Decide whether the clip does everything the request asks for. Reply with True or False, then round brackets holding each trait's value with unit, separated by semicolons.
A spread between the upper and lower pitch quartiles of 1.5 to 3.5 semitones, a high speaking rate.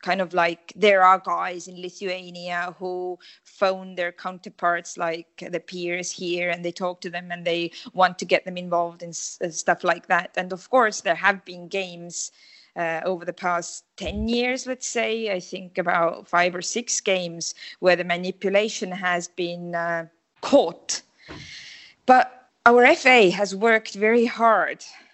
False (3.1 semitones; 165 wpm)